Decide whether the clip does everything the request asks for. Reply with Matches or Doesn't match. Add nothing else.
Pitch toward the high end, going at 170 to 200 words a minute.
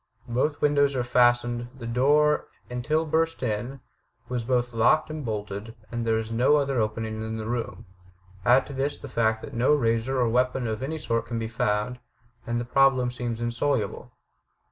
Doesn't match